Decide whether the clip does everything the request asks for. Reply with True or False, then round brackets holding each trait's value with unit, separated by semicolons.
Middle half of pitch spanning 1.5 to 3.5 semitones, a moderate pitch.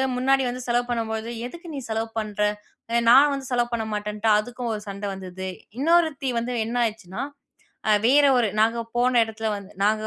False (2.9 semitones; 230 Hz)